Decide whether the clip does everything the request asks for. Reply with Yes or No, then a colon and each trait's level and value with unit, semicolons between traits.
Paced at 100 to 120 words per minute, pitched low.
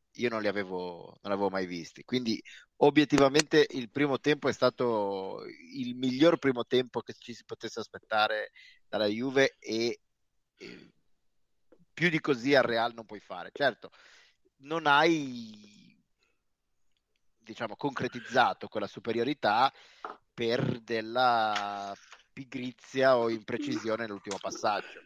Yes: slow, 115 wpm; low, 120 Hz